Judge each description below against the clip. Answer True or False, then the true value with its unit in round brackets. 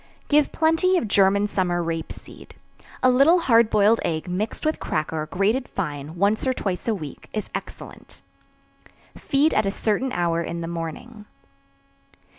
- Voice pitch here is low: False (205 Hz)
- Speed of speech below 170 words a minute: True (155 wpm)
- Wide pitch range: True (6.8 semitones)